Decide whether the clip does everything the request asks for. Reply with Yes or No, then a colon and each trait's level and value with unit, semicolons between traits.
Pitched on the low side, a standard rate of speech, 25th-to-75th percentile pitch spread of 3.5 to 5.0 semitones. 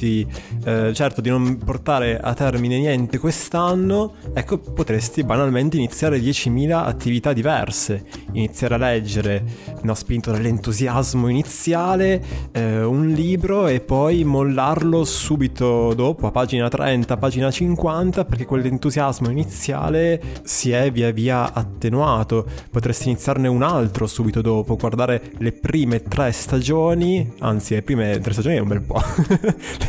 Yes: low, 125 Hz; average, 130 wpm; average, 4.7 semitones